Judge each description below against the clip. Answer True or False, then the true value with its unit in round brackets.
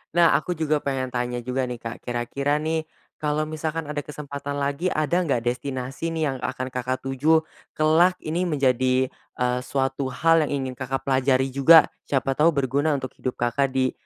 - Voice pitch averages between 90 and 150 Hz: True (140 Hz)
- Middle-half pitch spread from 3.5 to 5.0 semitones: False (3.1 semitones)